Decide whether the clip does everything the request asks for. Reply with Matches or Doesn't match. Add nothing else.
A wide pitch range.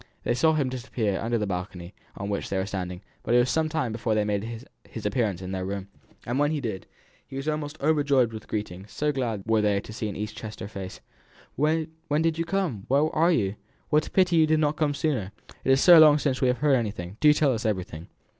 Matches